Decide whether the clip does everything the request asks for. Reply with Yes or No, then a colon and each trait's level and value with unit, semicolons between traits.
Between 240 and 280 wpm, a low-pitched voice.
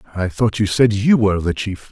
Yes: fast, 250 wpm; low, 105 Hz